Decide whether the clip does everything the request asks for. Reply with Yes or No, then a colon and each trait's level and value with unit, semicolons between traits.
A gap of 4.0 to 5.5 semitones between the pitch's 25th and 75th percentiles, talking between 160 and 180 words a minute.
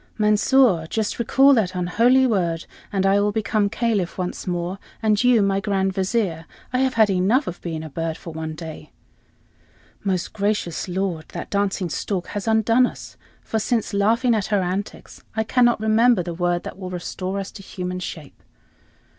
No: average, 3.6 semitones; average, 175 wpm